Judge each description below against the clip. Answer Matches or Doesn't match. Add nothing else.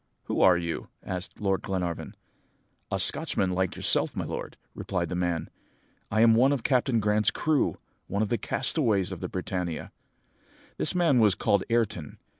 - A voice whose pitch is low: Matches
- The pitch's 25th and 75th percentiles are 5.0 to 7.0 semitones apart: Doesn't match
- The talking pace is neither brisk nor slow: Matches